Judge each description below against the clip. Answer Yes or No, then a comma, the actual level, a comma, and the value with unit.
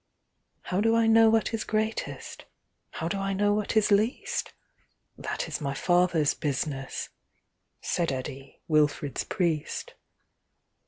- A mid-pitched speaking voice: Yes, medium, 180 Hz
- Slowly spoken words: Yes, slow, 110 wpm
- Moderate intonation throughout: No, wide, 6.4 semitones